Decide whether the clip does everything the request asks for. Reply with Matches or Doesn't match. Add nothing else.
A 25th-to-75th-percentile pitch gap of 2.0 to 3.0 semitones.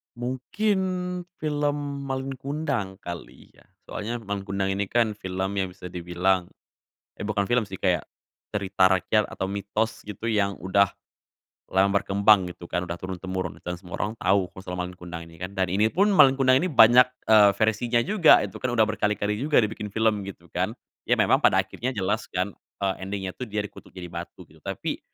Doesn't match